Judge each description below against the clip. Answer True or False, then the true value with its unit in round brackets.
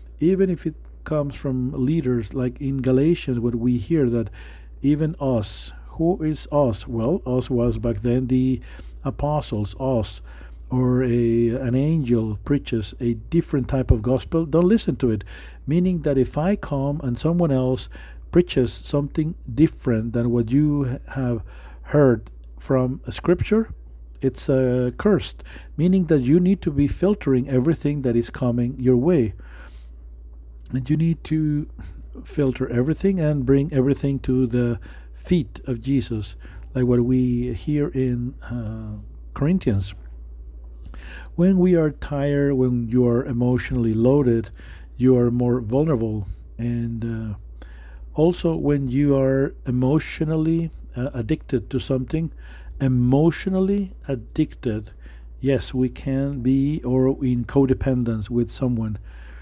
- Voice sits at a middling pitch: False (130 Hz)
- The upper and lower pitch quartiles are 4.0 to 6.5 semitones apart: True (4.3 semitones)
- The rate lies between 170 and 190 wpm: False (130 wpm)